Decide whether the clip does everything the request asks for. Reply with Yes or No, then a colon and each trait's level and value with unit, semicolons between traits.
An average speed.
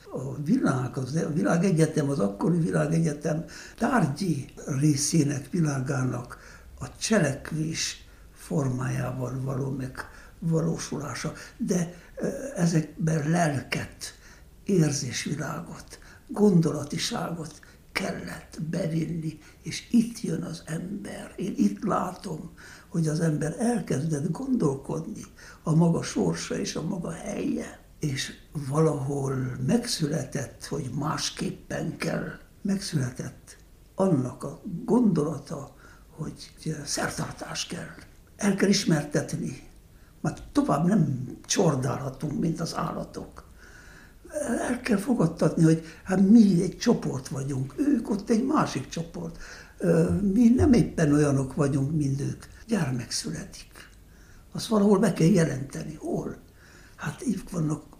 No: slow, 100 wpm